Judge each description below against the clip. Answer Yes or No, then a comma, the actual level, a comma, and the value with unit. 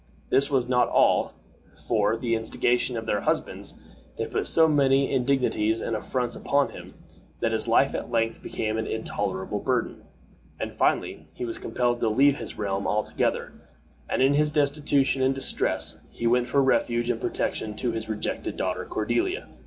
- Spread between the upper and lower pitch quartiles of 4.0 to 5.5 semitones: No, average, 3.4 semitones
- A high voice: No, low, 120 Hz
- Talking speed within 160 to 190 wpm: Yes, average, 170 wpm